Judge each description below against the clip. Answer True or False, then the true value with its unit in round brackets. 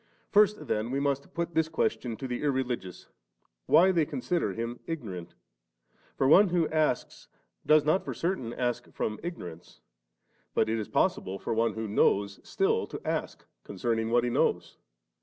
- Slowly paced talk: False (160 wpm)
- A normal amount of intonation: False (6.6 semitones)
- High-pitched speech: False (125 Hz)